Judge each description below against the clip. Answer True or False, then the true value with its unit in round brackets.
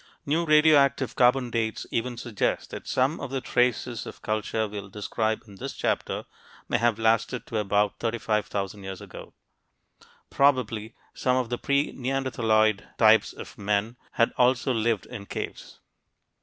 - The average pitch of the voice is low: True (115 Hz)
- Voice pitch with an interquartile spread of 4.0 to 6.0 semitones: False (2.9 semitones)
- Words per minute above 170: False (145 wpm)